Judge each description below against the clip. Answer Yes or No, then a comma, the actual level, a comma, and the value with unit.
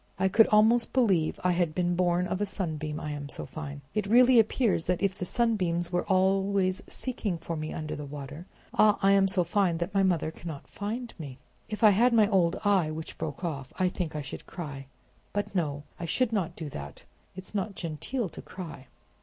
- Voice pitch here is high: No, medium, 180 Hz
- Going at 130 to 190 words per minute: No, fast, 205 wpm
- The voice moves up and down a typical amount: Yes, average, 4.6 semitones